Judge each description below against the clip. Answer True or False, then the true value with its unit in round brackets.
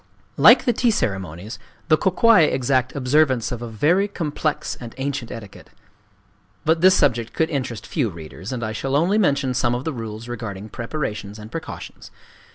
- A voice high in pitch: False (130 Hz)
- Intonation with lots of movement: True (5.7 semitones)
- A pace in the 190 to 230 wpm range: False (170 wpm)